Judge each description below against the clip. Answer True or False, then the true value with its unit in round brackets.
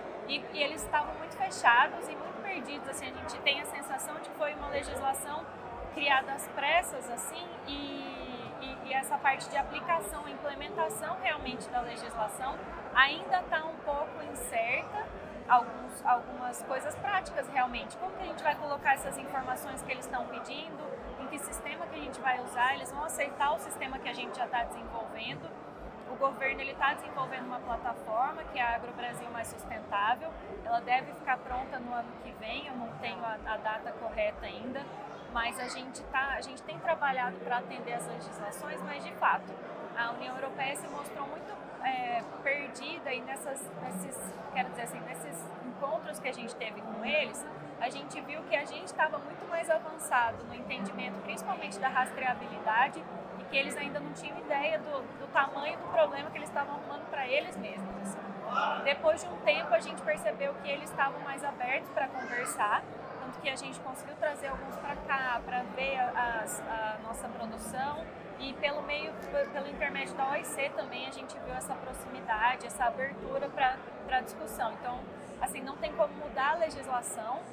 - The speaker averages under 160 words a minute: False (180 wpm)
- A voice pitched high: True (275 Hz)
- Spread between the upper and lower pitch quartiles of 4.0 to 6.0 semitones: False (3.6 semitones)